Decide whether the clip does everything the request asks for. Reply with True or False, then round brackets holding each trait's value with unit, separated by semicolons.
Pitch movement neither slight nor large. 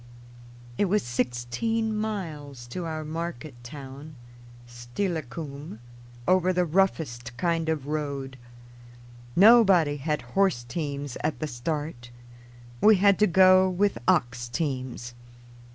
False (7.0 semitones)